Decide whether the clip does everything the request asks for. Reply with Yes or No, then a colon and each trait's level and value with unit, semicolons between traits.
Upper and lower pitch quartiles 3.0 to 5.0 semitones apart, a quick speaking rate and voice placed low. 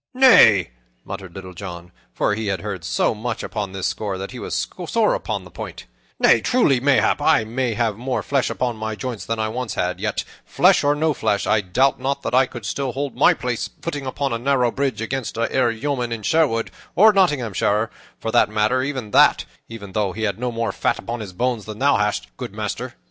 Yes: average, 4.1 semitones; fast, 215 wpm; low, 115 Hz